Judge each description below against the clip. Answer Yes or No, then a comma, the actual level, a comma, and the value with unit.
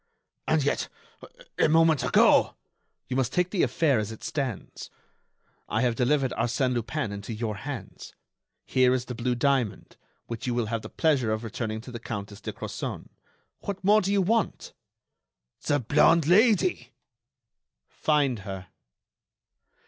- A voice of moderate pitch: No, low, 125 Hz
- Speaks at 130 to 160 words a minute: Yes, average, 150 wpm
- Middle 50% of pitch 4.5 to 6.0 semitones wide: Yes, average, 5.2 semitones